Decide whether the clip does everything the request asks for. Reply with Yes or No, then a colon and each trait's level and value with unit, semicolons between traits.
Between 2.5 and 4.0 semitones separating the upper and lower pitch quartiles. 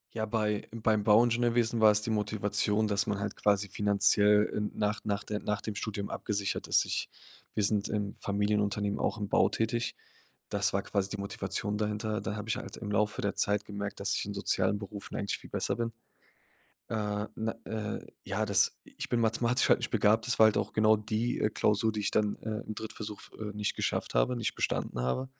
No: narrow, 1.2 semitones